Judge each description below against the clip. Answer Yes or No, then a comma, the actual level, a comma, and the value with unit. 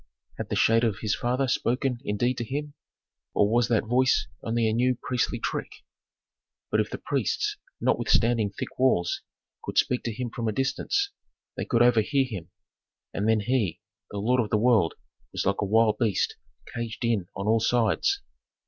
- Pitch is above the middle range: No, low, 115 Hz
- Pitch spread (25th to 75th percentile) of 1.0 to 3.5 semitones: Yes, average, 2.7 semitones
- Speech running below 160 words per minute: No, average, 175 wpm